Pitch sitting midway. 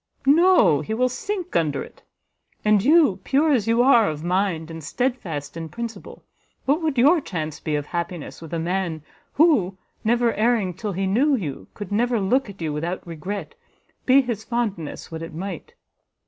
No: high, 200 Hz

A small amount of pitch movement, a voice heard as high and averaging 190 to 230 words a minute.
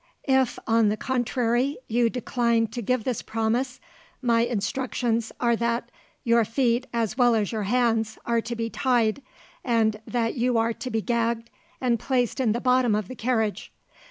No: narrow, 1.7 semitones; high, 235 Hz; average, 170 wpm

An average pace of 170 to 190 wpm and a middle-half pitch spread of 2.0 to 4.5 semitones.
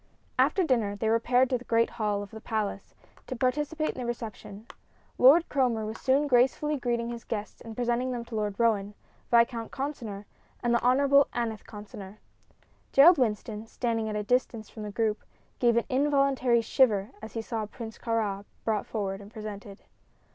Yes: average, 175 wpm; average, 3.0 semitones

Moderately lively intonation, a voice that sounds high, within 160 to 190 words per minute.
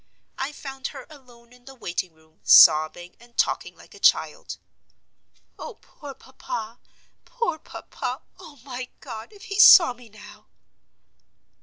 No: average, 5.0 semitones; very high, 250 Hz; average, 140 wpm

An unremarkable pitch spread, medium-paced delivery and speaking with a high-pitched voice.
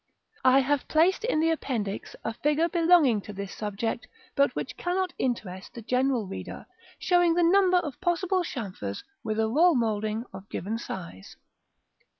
No: wide, 8.0 semitones; average, 160 wpm; very high, 255 Hz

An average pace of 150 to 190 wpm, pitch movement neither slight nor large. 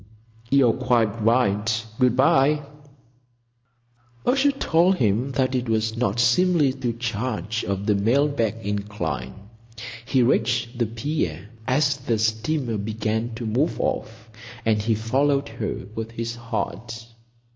No: slow, 135 wpm; average, 3.2 semitones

